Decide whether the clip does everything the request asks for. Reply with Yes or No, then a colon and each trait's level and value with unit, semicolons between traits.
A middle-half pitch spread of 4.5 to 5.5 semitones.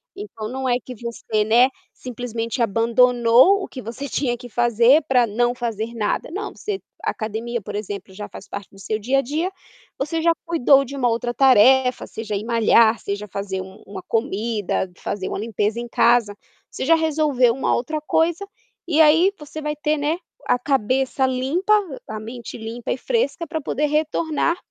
Yes: average, 5.0 semitones